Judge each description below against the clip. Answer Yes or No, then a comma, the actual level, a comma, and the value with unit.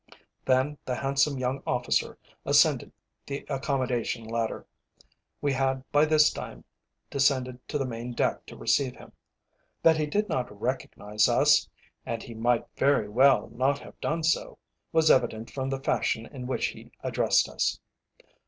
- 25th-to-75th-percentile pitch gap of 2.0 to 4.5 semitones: Yes, narrow, 2.4 semitones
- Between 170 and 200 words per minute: No, average, 155 wpm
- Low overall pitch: Yes, low, 130 Hz